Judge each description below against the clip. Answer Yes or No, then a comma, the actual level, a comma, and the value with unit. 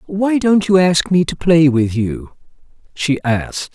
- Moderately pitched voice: Yes, medium, 160 Hz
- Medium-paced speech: Yes, average, 175 wpm